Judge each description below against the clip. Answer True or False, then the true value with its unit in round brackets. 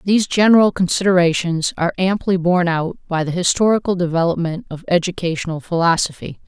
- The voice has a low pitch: False (175 Hz)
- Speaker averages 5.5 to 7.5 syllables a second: True (6.0 syllables/s)